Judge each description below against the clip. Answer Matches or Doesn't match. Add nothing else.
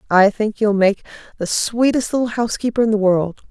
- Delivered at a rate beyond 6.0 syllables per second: Doesn't match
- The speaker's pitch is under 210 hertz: Doesn't match